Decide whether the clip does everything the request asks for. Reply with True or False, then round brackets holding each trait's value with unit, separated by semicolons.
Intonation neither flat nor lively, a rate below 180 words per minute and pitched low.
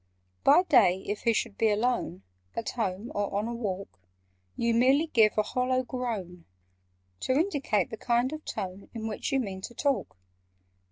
False (4.0 semitones; 170 wpm; 230 Hz)